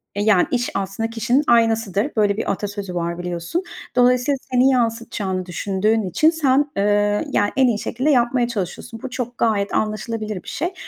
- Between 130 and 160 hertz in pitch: No, high, 225 Hz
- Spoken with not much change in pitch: No, average, 3.8 semitones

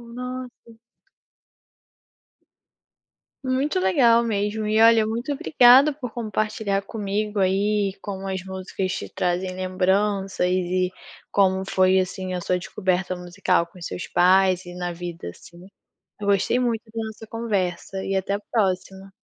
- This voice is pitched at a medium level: No, high, 195 Hz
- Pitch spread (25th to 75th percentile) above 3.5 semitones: No, average, 2.9 semitones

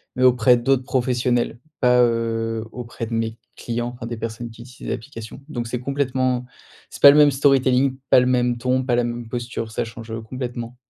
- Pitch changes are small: Yes, narrow, 1.7 semitones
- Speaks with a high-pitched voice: No, low, 120 Hz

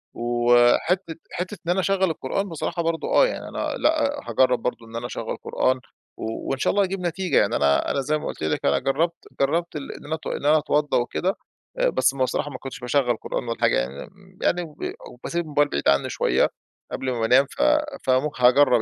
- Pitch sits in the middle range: Yes, medium, 145 Hz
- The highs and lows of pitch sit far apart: Yes, wide, 6.1 semitones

